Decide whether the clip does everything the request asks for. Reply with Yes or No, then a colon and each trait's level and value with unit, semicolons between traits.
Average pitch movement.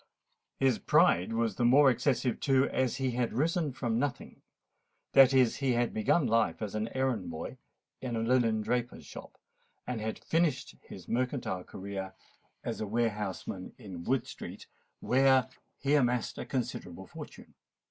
Yes: average, 3.3 semitones